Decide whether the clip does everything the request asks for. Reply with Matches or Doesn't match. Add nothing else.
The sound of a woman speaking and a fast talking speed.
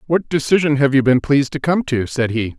Doesn't match